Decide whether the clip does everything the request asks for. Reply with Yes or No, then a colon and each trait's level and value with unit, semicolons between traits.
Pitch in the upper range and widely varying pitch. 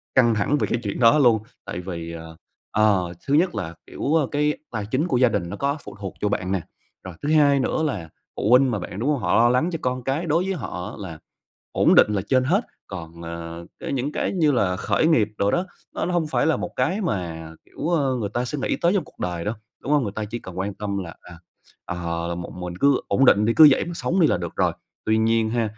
No: low, 115 Hz; wide, 7.8 semitones